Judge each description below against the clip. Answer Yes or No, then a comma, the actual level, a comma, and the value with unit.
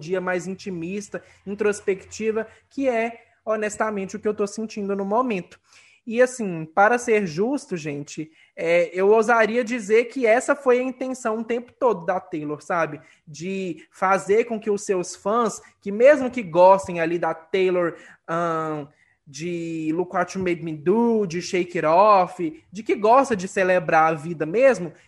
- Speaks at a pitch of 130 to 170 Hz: No, high, 195 Hz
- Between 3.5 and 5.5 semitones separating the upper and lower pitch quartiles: Yes, average, 4.5 semitones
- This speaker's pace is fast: No, average, 165 wpm